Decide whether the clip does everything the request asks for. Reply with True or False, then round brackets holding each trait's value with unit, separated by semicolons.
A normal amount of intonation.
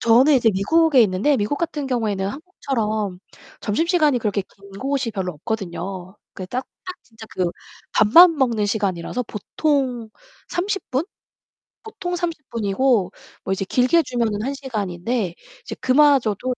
False (6.0 semitones)